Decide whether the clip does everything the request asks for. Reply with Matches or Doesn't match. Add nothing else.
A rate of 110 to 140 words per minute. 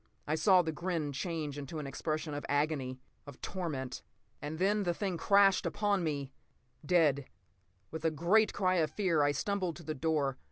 Doesn't match